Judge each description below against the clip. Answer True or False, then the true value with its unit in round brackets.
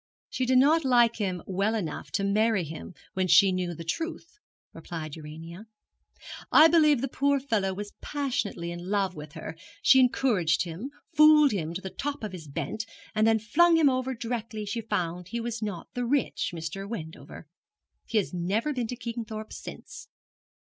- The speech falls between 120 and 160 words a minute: False (175 wpm)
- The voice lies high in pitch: True (215 Hz)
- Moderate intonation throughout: False (6.1 semitones)